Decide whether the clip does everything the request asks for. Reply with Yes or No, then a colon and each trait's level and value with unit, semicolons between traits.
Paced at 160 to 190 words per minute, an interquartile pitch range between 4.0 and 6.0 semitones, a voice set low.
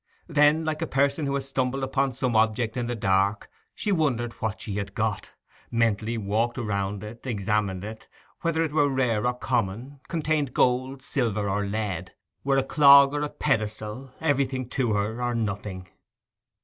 Yes: average, 170 wpm; average, 4.4 semitones; low, 120 Hz